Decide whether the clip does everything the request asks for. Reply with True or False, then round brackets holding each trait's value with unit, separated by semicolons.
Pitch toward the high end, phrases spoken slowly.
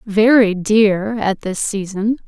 True (210 Hz; 130 wpm)